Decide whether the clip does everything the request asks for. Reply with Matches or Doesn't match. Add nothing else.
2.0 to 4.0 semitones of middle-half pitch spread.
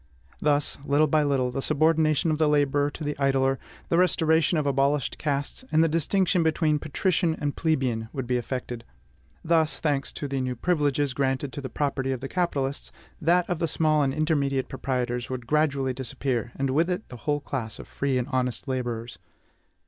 Matches